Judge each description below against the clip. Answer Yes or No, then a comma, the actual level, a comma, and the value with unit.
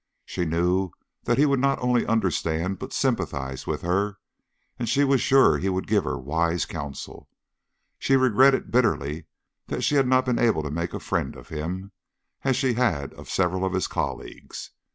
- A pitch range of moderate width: No, wide, 7.2 semitones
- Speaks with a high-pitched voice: No, very low, 95 Hz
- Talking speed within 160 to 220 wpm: Yes, average, 180 wpm